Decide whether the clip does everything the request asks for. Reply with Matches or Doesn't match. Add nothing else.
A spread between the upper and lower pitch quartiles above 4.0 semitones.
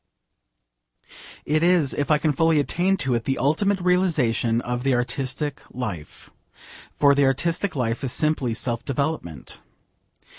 Matches